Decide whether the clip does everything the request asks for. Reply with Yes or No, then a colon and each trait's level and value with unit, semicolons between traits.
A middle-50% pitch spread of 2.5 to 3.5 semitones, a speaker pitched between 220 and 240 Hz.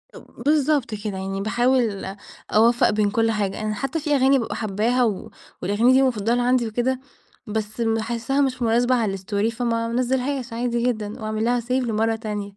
Yes: average, 2.8 semitones; high, 230 Hz